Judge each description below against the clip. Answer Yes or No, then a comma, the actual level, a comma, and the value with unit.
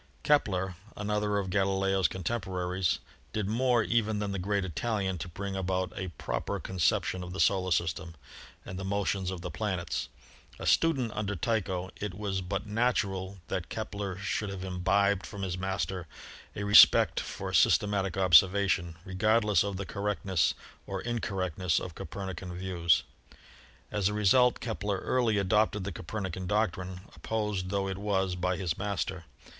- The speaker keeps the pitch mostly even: Yes, narrow, 2.0 semitones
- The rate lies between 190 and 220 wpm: No, average, 155 wpm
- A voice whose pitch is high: No, very low, 95 Hz